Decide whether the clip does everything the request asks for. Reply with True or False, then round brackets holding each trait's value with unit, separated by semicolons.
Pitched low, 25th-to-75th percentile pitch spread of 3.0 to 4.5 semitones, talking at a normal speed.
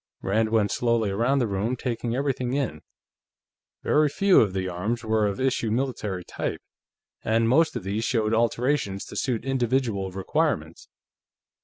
True (115 Hz; 4.0 semitones; 150 wpm)